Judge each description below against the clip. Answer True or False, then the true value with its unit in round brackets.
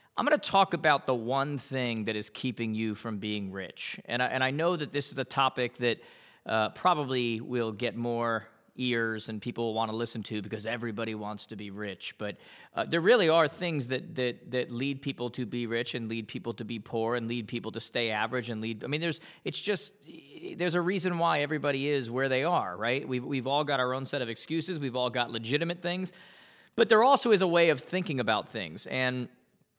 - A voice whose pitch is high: False (125 Hz)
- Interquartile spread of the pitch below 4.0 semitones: False (4.4 semitones)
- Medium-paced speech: False (230 wpm)